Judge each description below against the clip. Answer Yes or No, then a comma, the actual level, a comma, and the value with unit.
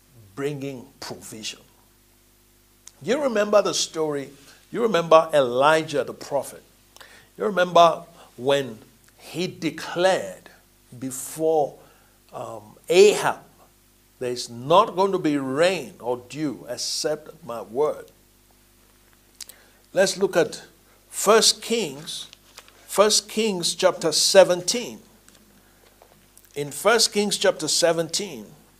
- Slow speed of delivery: Yes, slow, 90 wpm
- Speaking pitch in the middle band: Yes, medium, 155 Hz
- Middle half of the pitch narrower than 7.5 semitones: No, wide, 8.2 semitones